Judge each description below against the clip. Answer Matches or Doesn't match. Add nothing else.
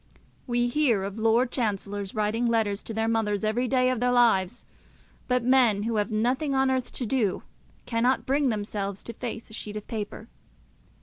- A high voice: Matches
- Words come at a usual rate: Matches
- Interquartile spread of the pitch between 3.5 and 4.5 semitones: Doesn't match